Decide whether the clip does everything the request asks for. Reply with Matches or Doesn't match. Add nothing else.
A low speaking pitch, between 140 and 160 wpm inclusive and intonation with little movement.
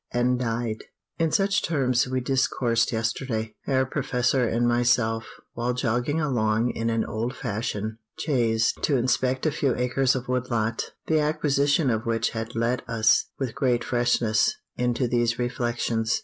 Matches